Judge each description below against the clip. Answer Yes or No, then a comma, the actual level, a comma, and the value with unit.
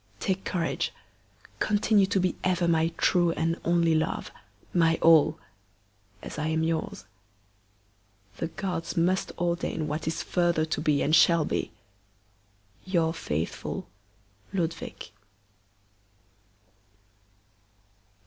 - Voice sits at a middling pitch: Yes, medium, 165 Hz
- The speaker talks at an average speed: No, slow, 105 wpm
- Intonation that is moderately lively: No, narrow, 2.0 semitones